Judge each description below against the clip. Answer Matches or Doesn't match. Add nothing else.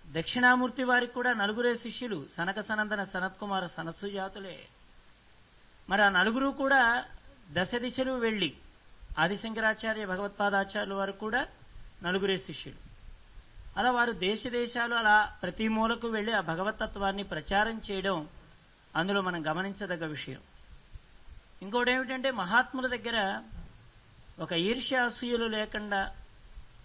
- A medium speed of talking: Doesn't match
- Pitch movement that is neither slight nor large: Matches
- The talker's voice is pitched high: Matches